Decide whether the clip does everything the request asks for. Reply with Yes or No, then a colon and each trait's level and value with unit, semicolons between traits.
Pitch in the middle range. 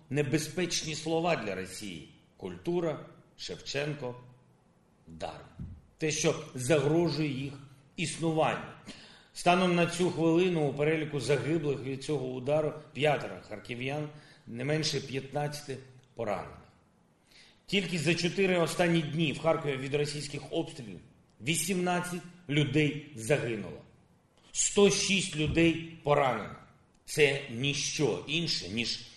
Yes: medium, 150 Hz